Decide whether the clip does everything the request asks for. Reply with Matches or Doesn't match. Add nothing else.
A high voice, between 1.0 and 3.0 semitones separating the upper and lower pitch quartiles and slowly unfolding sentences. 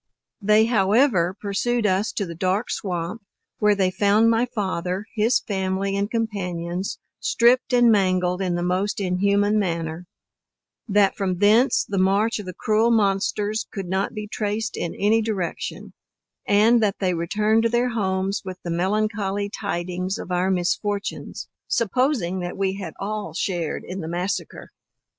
Doesn't match